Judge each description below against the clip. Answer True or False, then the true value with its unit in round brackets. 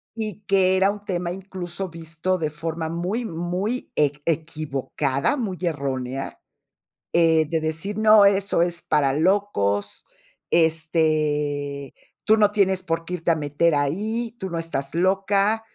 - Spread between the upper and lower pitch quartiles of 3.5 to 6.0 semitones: True (4.2 semitones)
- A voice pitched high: False (170 Hz)